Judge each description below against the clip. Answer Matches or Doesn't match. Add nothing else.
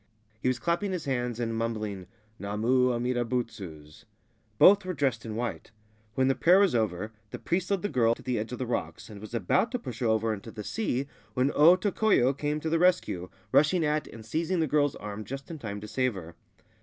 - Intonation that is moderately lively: Doesn't match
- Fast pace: Matches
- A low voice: Matches